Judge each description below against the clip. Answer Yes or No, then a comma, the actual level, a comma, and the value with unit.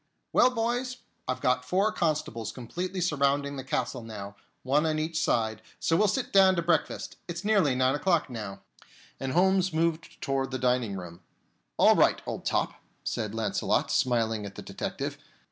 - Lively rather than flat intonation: Yes, wide, 7.2 semitones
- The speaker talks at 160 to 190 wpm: Yes, average, 165 wpm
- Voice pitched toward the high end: No, medium, 140 Hz